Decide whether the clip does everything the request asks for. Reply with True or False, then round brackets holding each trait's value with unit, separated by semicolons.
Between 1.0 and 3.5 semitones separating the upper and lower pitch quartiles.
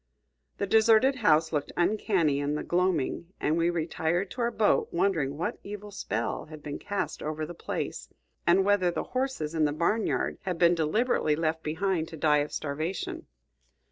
False (4.7 semitones)